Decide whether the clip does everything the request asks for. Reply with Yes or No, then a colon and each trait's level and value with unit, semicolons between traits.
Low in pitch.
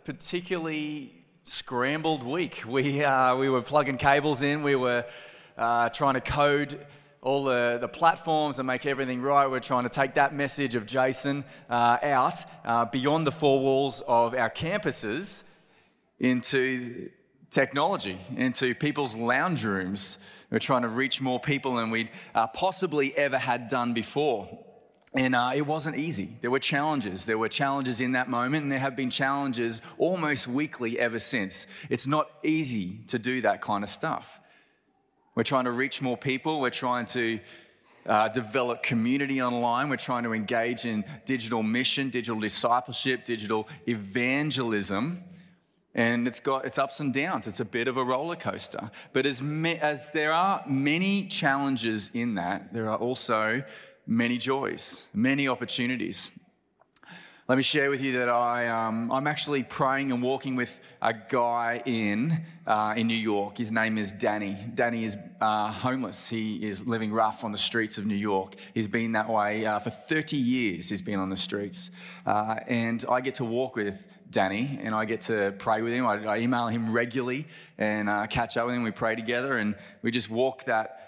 Yes: low, 125 Hz